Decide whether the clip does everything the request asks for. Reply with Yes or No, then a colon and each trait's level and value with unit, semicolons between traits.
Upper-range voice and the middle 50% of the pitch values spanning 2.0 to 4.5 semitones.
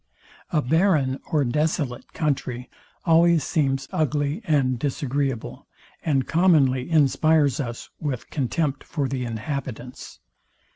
No: medium, 140 Hz; average, 3.3 semitones